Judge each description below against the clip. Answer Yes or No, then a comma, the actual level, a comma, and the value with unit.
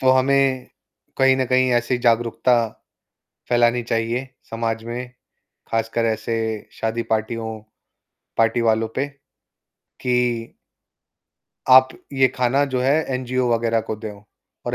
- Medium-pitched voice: No, low, 120 Hz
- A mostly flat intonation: Yes, narrow, 2.1 semitones